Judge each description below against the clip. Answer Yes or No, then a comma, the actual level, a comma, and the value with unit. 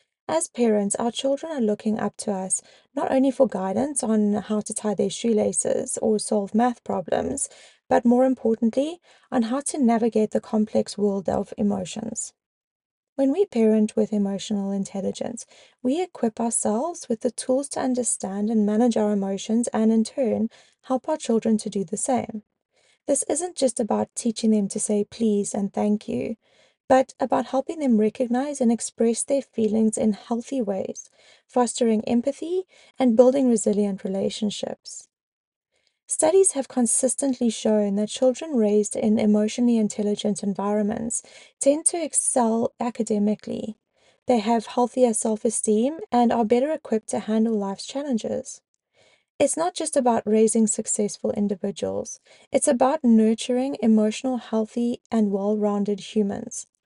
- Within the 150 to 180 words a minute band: No, average, 140 wpm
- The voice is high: Yes, high, 230 Hz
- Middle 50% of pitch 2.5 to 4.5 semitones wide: Yes, average, 3.3 semitones